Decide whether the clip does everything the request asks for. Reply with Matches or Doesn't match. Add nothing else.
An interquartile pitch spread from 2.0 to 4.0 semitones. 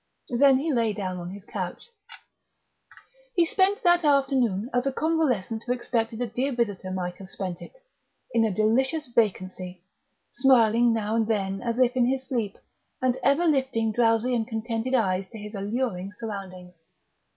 Doesn't match